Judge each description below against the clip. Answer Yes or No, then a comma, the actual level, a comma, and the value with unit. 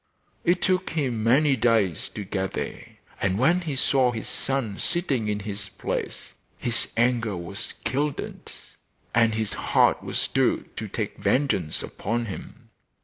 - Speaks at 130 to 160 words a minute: Yes, average, 145 wpm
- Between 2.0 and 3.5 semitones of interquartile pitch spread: No, average, 4.8 semitones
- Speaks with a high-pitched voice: No, low, 115 Hz